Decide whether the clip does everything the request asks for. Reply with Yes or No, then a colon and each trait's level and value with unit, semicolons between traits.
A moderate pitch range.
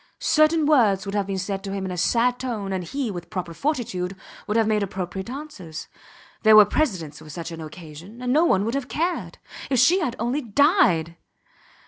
No: wide, 6.2 semitones